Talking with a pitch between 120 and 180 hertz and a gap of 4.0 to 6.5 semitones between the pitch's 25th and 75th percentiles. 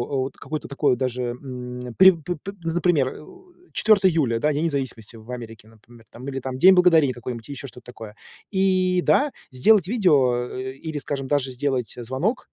Yes: low, 135 Hz; wide, 5.4 semitones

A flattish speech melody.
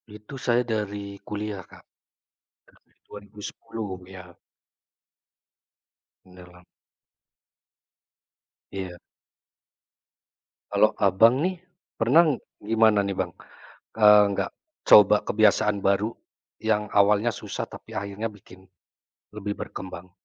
Yes: narrow, 2.2 semitones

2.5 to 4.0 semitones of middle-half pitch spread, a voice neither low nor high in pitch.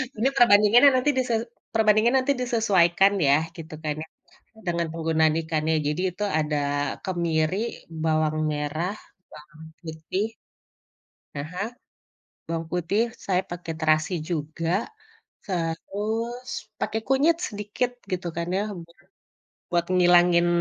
No: average, 4.7 semitones; medium, 175 Hz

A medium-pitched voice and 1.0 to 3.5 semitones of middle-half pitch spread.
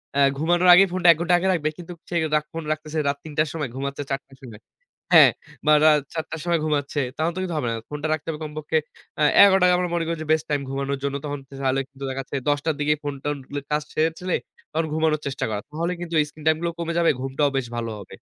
Yes: medium, 155 Hz; average, 2.8 semitones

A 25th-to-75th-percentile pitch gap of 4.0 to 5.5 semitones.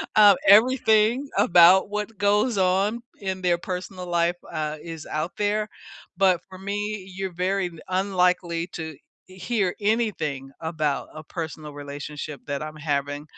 Yes: average, 4.3 semitones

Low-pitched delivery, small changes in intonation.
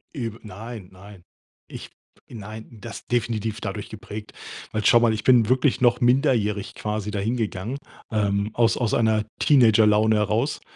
Yes: low, 110 Hz; narrow, 2.1 semitones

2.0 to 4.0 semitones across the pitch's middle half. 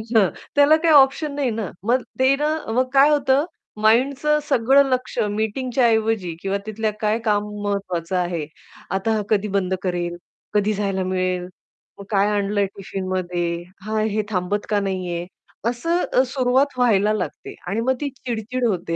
No: average, 4.9 semitones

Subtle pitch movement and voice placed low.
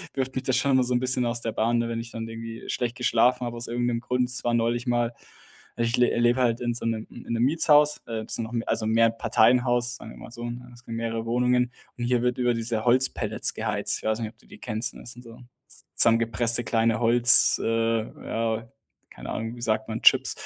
Yes: narrow, 1.3 semitones; low, 120 Hz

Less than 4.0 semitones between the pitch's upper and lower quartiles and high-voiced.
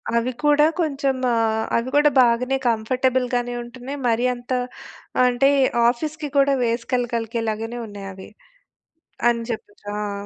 Yes: narrow, 2.4 semitones; high, 245 Hz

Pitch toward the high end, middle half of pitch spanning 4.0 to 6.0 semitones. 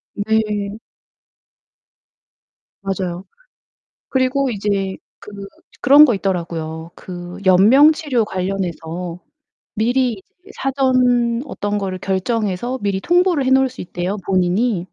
Yes: high, 205 Hz; wide, 5.5 semitones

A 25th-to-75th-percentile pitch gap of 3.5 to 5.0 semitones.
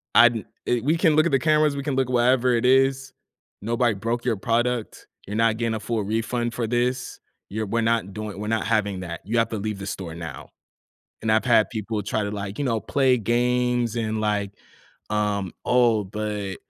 No: average, 2.7 semitones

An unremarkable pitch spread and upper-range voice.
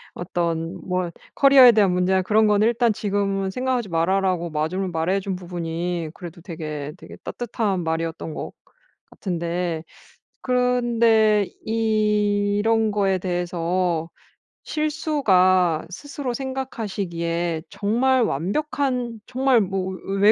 Yes: average, 4.7 semitones; high, 195 Hz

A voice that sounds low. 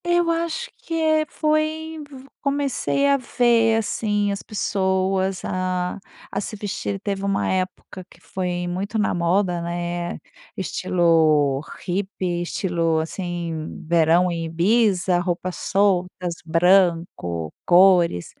No: medium, 185 Hz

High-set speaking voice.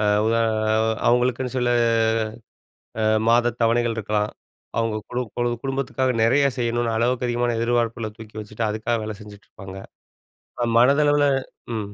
No: low, 120 Hz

